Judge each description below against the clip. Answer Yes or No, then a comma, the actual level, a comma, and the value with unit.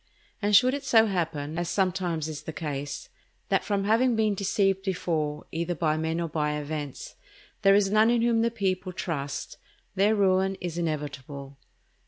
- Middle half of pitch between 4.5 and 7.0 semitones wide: Yes, average, 4.9 semitones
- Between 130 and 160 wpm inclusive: No, average, 170 wpm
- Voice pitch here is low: No, medium, 180 Hz